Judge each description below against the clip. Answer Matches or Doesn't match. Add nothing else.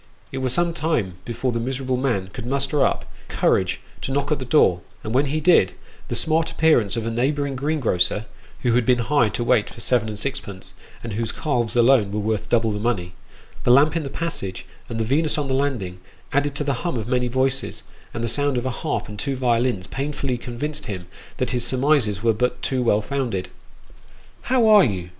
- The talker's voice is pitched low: Matches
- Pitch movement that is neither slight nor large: Matches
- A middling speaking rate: Doesn't match